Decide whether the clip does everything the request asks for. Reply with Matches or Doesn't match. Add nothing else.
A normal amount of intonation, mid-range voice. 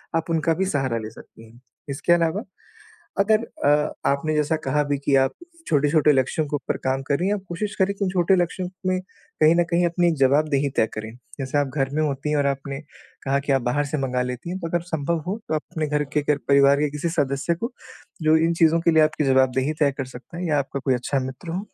Matches